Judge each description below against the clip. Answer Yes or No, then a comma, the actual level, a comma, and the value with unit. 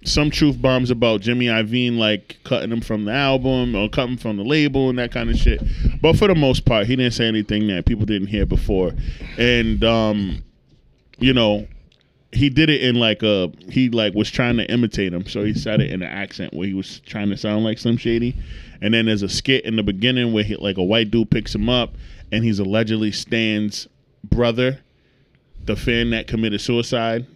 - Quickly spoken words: Yes, fast, 210 wpm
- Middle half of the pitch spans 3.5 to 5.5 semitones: No, average, 2.9 semitones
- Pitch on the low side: Yes, low, 115 Hz